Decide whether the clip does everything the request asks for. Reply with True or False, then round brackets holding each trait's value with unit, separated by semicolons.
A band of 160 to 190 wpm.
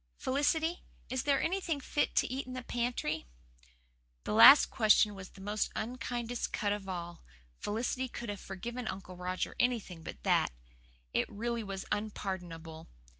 False (150 wpm)